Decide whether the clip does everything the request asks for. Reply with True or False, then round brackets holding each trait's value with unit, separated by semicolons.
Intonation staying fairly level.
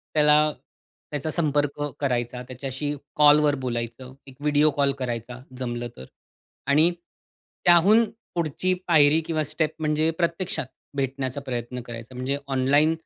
False (3.2 semitones)